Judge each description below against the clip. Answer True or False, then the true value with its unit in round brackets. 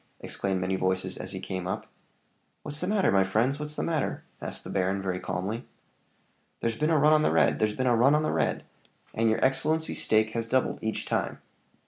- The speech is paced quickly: True (210 wpm)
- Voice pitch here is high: False (115 Hz)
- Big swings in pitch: True (7.5 semitones)